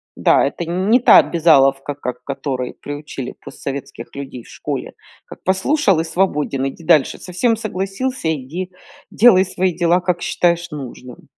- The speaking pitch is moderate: Yes, medium, 170 Hz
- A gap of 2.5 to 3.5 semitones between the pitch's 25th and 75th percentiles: No, average, 5.2 semitones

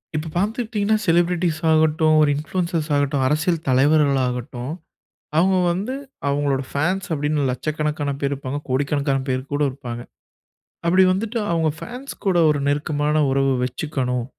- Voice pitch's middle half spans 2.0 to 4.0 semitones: Yes, average, 3.7 semitones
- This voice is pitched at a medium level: Yes, medium, 150 Hz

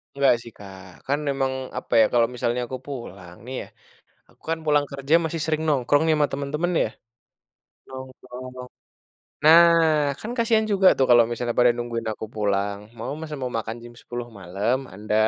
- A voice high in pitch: No, low, 125 Hz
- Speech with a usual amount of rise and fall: Yes, average, 4.0 semitones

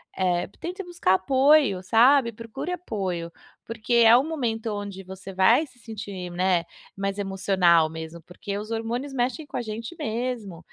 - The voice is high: Yes, high, 215 Hz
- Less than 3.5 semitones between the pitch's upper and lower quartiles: No, average, 4.8 semitones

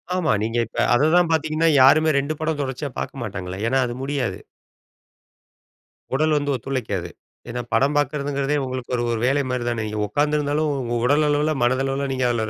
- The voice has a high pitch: No, medium, 140 Hz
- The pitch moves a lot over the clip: No, average, 3.3 semitones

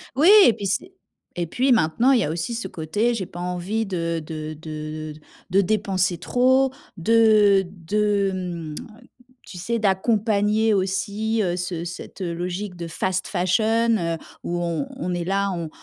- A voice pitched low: No, high, 190 Hz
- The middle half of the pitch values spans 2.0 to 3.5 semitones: No, average, 4.0 semitones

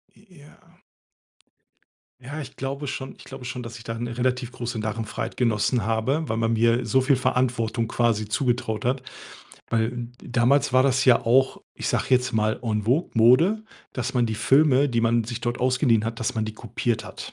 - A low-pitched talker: Yes, low, 120 Hz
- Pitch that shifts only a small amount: Yes, narrow, 2.3 semitones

